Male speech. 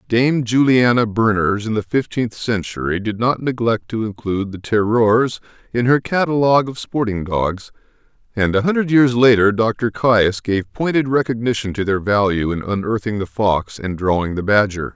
Yes: male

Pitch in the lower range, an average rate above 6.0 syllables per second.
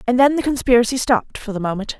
No: high, 240 Hz; 7.1 syllables/s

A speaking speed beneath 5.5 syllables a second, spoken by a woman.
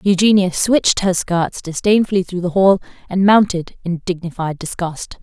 Yes: 4.9 syllables/s; female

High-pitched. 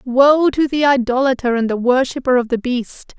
Yes: very high, 255 Hz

